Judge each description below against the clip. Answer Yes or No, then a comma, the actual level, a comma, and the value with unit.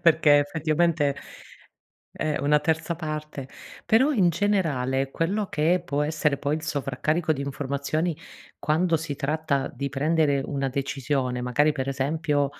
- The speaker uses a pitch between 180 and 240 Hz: No, medium, 150 Hz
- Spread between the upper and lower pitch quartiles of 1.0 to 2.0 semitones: No, narrow, 2.5 semitones